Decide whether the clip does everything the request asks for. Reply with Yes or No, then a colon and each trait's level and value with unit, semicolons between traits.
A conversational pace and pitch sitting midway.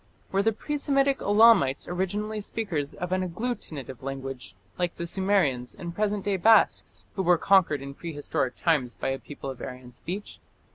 Yes: average, 165 wpm; medium, 175 Hz